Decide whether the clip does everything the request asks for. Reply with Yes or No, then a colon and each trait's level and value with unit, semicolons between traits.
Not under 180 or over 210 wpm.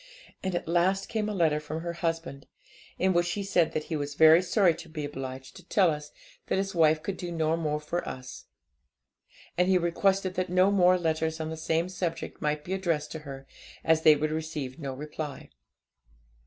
Yes: average, 200 wpm